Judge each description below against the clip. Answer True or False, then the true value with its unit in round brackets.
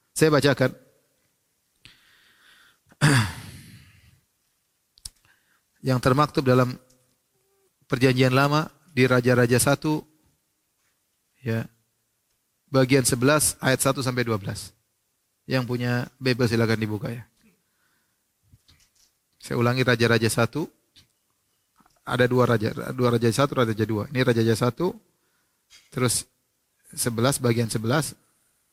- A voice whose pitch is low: True (125 Hz)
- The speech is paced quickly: False (85 wpm)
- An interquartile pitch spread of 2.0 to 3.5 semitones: True (2.7 semitones)